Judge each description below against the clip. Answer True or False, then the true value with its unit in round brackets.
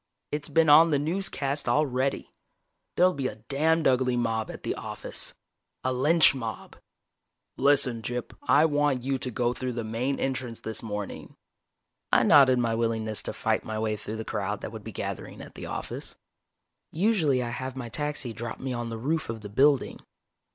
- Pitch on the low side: True (125 Hz)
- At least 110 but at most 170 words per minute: False (180 wpm)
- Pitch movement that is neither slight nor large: True (4.2 semitones)